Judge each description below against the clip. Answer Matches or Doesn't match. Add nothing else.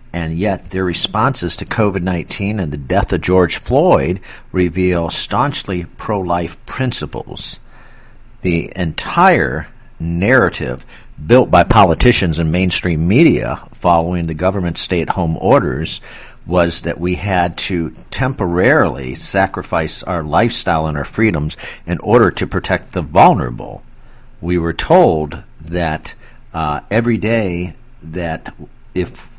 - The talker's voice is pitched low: Matches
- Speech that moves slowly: Matches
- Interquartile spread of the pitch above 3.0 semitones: Doesn't match